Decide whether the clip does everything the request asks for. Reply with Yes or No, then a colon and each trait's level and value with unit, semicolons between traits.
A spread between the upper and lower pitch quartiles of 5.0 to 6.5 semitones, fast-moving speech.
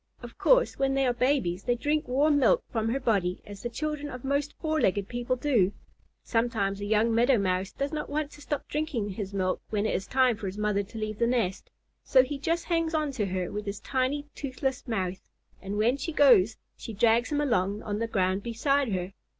Yes: wide, 5.6 semitones; fast, 220 wpm